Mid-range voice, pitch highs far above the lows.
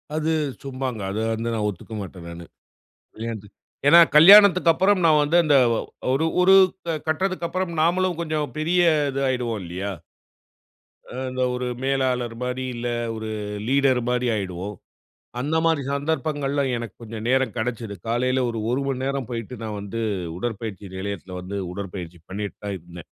No: low, 125 Hz; wide, 6.1 semitones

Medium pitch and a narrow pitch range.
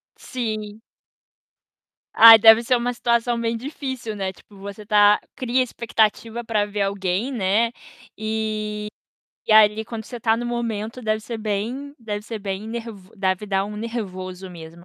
No: high, 220 Hz; narrow, 2.2 semitones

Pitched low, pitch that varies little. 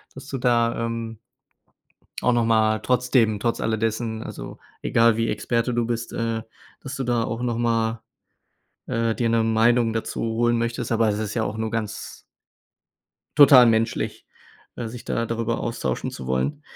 Yes: low, 115 Hz; narrow, 1.0 semitones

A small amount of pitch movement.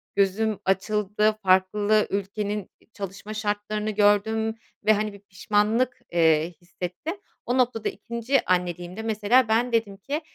Yes: narrow, 2.3 semitones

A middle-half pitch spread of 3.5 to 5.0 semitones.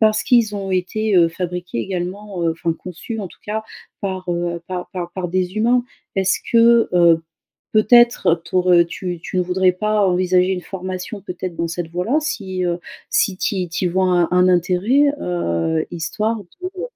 No: average, 2.8 semitones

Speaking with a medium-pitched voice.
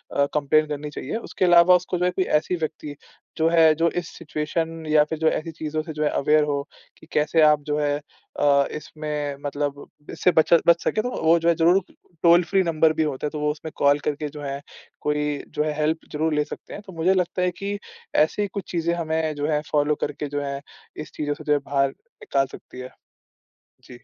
Yes: medium, 155 Hz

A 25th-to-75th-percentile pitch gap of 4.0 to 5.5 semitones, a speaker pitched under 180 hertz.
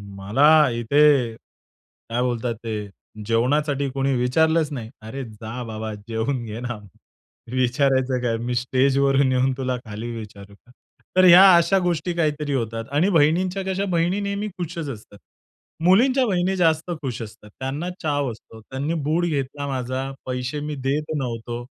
Yes: average, 5.0 semitones; low, 135 Hz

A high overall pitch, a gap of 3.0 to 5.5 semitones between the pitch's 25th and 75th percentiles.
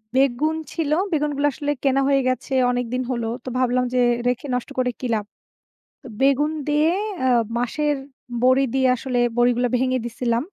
No: very high, 255 Hz; narrow, 2.5 semitones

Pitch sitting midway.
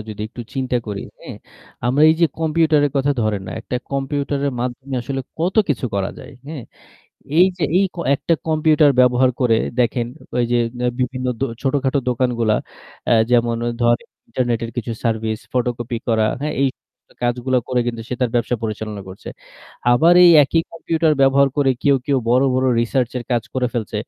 No: low, 125 Hz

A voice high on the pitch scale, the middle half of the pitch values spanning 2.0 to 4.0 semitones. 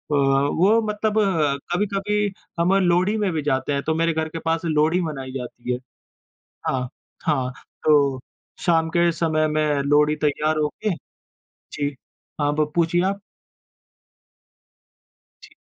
No: medium, 155 Hz; average, 3.6 semitones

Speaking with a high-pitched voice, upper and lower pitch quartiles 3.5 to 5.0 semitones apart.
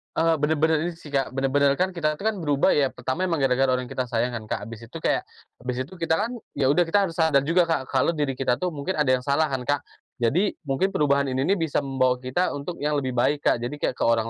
No: medium, 140 Hz; average, 4.0 semitones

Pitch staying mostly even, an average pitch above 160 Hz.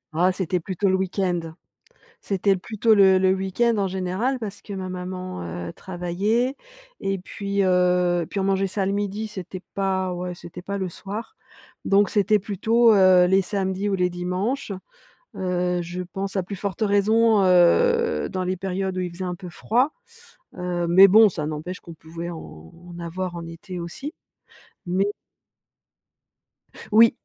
Yes: narrow, 2.1 semitones; high, 190 Hz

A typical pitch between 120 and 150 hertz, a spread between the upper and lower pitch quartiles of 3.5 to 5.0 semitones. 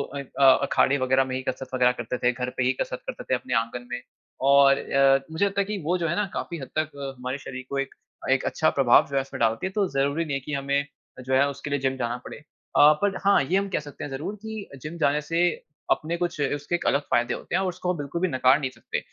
Yes: medium, 140 Hz; average, 4.4 semitones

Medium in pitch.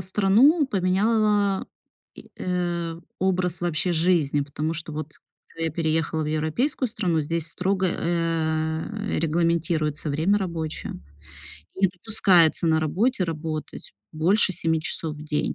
Yes: medium, 170 Hz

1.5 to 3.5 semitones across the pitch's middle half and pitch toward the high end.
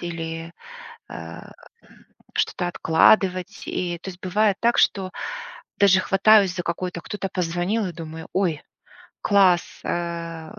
No: narrow, 2.5 semitones; medium, 180 Hz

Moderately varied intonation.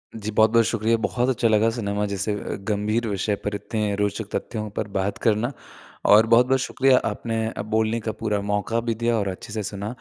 No: narrow, 1.9 semitones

